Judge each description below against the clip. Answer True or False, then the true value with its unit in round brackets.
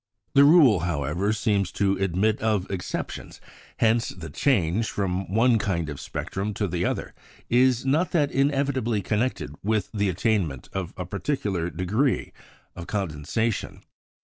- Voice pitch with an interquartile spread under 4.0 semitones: False (4.7 semitones)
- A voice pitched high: False (100 Hz)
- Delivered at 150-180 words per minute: False (135 wpm)